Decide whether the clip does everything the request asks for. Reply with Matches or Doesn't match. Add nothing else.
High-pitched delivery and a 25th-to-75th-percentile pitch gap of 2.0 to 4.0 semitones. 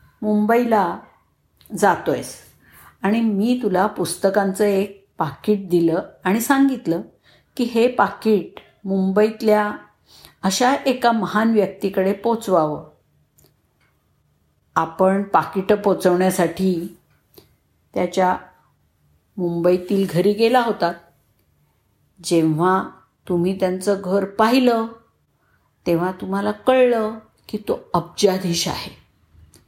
Matches